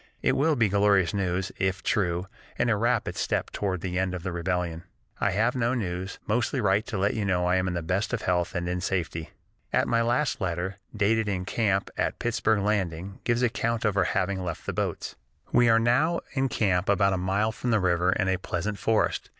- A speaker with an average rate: No, fast, 215 wpm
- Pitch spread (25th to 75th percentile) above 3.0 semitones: Yes, average, 3.7 semitones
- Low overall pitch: Yes, low, 100 Hz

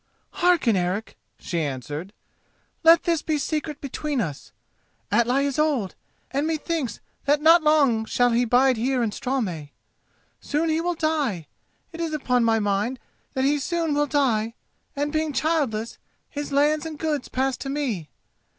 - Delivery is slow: No, average, 160 wpm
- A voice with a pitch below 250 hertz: No, very high, 275 Hz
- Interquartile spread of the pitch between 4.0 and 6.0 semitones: Yes, average, 5.3 semitones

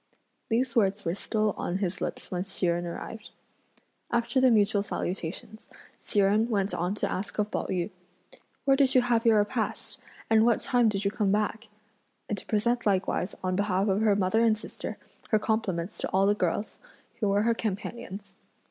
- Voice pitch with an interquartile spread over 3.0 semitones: No, average, 2.7 semitones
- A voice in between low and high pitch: No, high, 210 Hz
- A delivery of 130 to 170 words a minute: No, average, 185 wpm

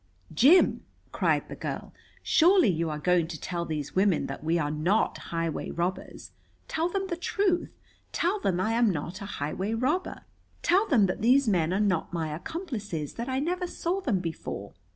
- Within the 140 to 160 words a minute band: No, average, 180 wpm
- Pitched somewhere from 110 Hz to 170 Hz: No, high, 200 Hz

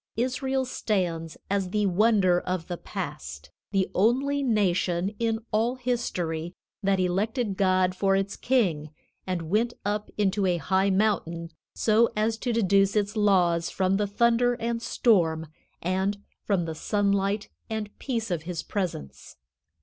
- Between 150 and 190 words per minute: No, average, 140 wpm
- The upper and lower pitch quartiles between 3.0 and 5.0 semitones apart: Yes, average, 3.7 semitones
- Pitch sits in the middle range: No, high, 200 Hz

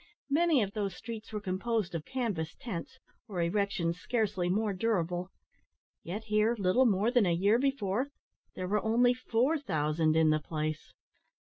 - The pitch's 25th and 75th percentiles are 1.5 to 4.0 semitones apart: No, average, 4.8 semitones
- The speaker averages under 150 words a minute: No, average, 155 wpm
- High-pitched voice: Yes, high, 205 Hz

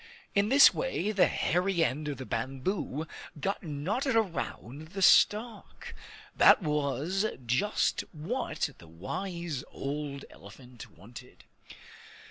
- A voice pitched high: No, medium, 160 Hz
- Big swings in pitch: Yes, wide, 6.6 semitones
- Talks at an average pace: No, slow, 110 wpm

